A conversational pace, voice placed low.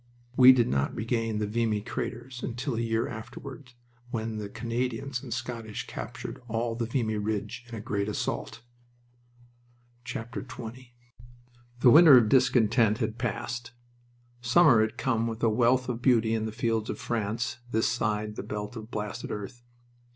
Yes: average, 155 wpm; low, 115 Hz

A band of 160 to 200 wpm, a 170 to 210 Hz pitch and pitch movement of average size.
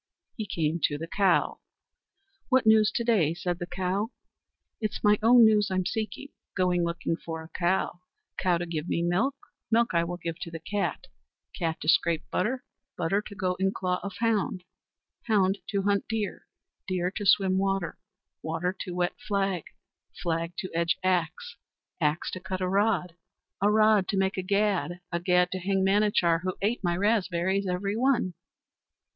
Yes: average, 175 wpm; medium, 185 Hz; average, 3.0 semitones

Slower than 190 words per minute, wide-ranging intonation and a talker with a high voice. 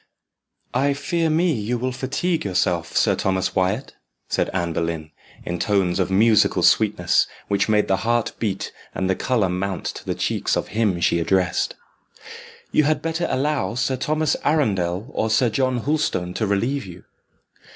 No: average, 160 wpm; wide, 6.3 semitones; low, 110 Hz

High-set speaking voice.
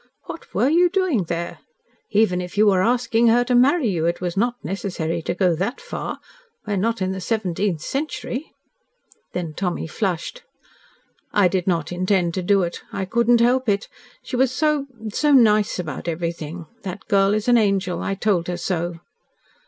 Yes: high, 195 Hz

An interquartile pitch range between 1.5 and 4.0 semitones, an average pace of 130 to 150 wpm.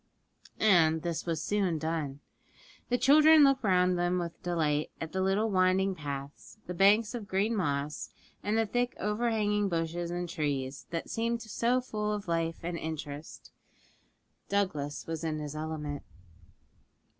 No: average, 4.8 semitones; average, 145 wpm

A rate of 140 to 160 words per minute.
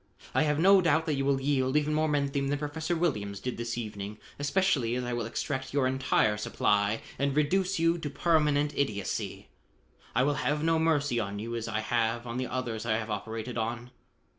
No: average, 200 wpm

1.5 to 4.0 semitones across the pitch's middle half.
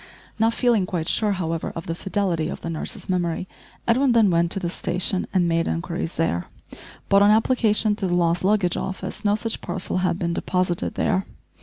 Yes: average, 3.5 semitones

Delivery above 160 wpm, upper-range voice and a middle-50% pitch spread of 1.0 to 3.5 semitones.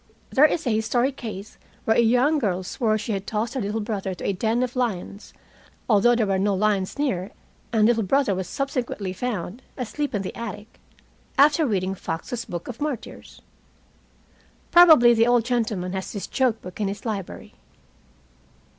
No: average, 170 wpm; high, 220 Hz; average, 4.0 semitones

